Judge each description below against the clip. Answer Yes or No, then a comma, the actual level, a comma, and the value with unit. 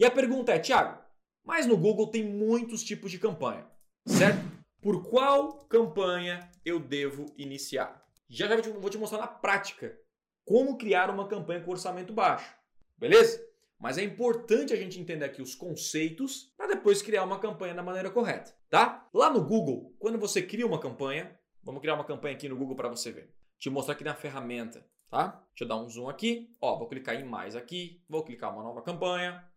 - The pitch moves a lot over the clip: Yes, wide, 6.6 semitones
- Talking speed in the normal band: No, fast, 195 wpm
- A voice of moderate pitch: No, high, 195 Hz